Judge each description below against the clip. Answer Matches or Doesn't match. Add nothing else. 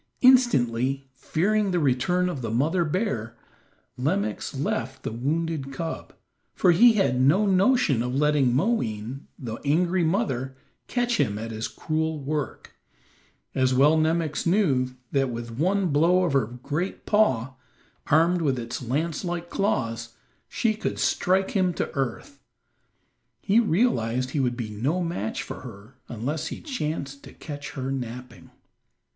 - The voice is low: Doesn't match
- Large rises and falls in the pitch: Matches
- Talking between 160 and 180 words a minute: Doesn't match